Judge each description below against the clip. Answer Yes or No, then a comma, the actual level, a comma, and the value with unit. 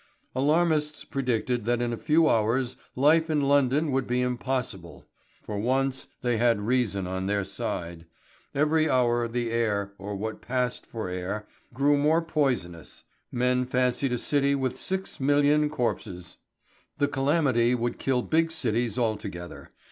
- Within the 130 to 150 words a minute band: Yes, average, 145 wpm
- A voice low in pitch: Yes, low, 125 Hz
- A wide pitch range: No, average, 4.4 semitones